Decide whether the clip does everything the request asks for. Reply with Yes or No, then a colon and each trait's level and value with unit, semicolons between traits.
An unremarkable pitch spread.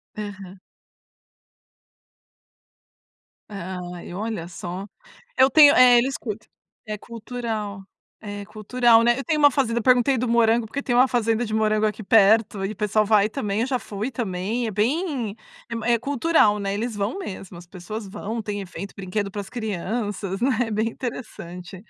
Yes: average, 3.2 semitones